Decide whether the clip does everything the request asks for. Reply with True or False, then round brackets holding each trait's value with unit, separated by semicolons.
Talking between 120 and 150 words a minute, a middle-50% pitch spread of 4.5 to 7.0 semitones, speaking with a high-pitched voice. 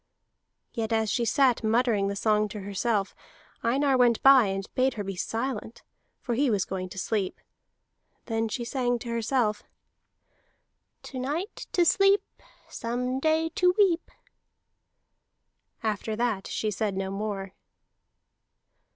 False (135 wpm; 4.0 semitones; 230 Hz)